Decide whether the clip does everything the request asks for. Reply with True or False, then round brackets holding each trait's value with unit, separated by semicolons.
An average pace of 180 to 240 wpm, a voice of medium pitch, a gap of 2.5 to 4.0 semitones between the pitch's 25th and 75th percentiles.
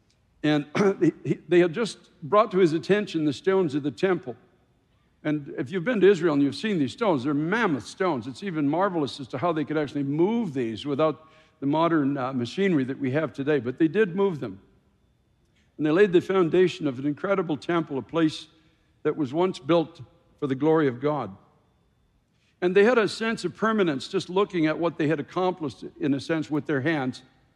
False (200 wpm; 155 Hz; 4.4 semitones)